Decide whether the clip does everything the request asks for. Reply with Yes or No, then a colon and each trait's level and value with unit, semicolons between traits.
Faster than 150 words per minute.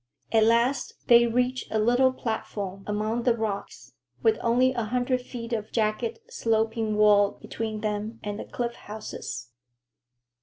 No: average, 145 wpm